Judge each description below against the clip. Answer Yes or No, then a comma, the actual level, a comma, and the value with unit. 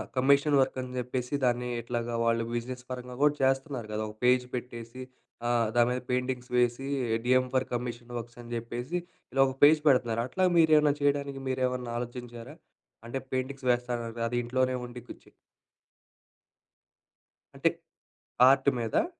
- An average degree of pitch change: No, narrow, 1.9 semitones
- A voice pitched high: No, low, 125 Hz